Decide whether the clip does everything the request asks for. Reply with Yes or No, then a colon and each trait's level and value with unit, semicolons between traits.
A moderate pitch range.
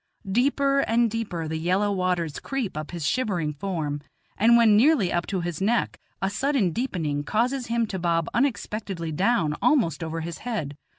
No: wide, 6.2 semitones